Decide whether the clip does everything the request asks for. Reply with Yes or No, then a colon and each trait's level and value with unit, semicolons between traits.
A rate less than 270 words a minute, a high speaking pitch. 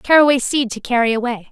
Yes: average, 200 wpm; very high, 250 Hz